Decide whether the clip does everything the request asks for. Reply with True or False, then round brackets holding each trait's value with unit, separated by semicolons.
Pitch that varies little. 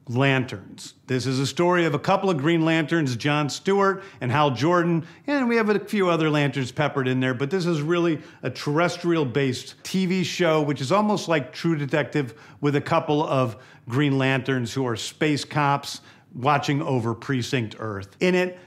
False (4.2 semitones)